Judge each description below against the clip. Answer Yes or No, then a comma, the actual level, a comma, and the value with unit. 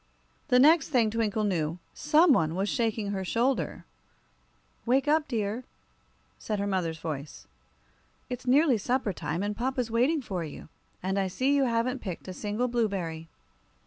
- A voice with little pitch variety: No, average, 5.2 semitones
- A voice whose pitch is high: Yes, high, 225 Hz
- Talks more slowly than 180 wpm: Yes, average, 155 wpm